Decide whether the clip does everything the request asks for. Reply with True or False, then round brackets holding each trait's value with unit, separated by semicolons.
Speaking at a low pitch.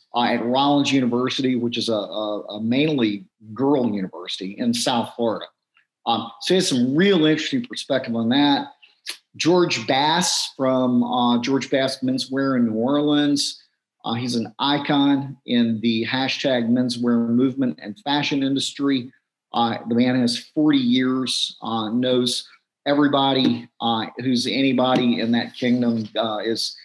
True (125 Hz)